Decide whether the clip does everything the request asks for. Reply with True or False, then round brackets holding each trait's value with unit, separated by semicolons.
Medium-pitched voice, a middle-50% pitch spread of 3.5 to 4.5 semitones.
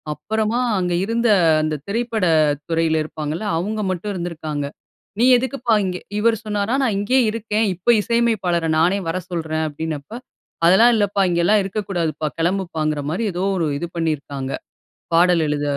False (180 Hz; 5.3 semitones)